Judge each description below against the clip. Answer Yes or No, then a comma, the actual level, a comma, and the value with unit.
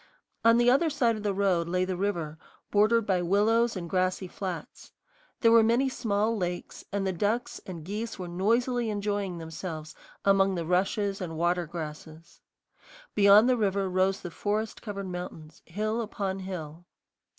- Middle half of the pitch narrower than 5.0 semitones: Yes, average, 3.4 semitones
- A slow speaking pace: No, average, 160 wpm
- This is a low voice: No, high, 195 Hz